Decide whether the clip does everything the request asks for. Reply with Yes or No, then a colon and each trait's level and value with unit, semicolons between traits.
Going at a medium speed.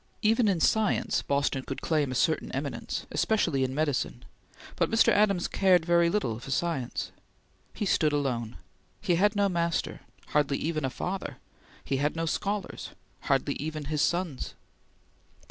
Yes: average, 150 wpm